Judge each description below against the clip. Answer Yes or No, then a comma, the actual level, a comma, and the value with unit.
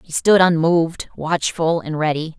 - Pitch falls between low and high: Yes, medium, 165 Hz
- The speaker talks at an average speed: Yes, average, 150 wpm